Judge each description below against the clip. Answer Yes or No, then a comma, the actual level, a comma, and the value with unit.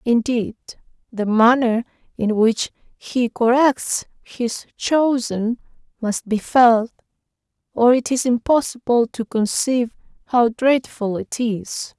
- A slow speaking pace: Yes, slow, 110 wpm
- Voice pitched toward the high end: Yes, high, 235 Hz